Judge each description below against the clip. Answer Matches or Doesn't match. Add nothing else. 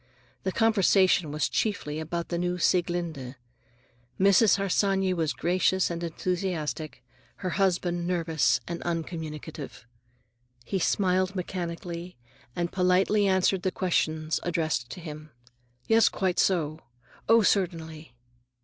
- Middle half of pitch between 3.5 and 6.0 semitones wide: Doesn't match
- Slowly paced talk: Matches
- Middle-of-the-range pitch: Matches